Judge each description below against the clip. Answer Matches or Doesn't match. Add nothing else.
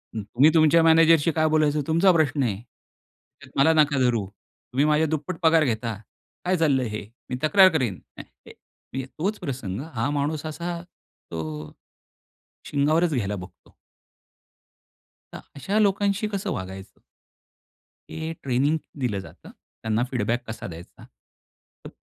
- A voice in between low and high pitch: Matches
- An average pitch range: Doesn't match